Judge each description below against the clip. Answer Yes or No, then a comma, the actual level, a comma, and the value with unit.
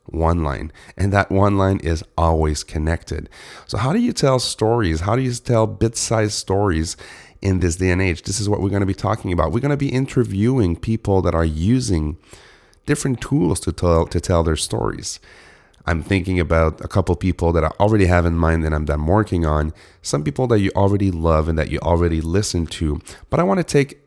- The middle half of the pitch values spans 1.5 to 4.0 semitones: No, average, 4.9 semitones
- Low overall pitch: Yes, very low, 95 Hz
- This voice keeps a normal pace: No, fast, 215 wpm